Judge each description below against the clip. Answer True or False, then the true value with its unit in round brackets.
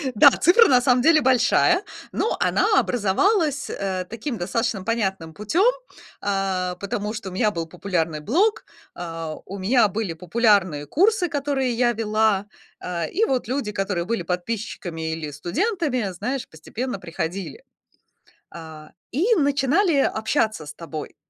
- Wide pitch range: True (7.2 semitones)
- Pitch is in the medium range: False (215 Hz)